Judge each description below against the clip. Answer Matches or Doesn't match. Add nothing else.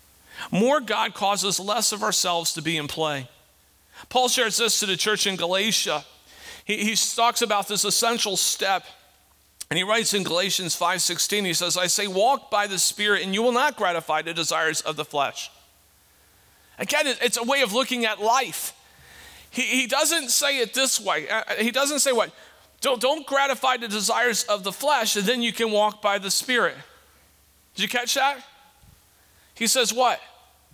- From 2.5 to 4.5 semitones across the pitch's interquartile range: Doesn't match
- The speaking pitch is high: Matches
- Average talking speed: Matches